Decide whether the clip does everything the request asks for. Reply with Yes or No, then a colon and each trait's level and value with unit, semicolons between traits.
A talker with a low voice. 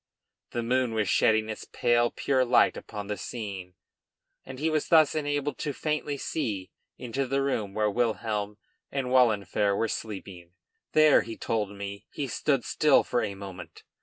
Yes: low, 115 Hz